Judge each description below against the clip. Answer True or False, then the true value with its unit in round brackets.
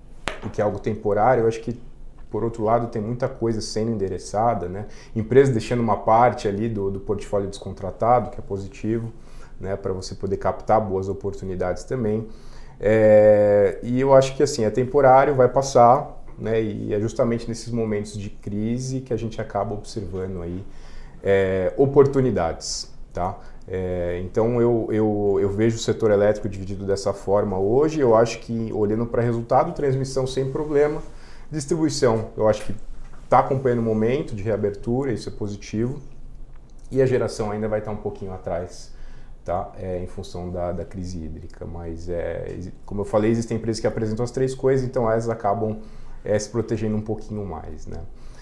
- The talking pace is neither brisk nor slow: True (175 wpm)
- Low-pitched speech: True (110 Hz)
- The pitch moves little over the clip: False (3.7 semitones)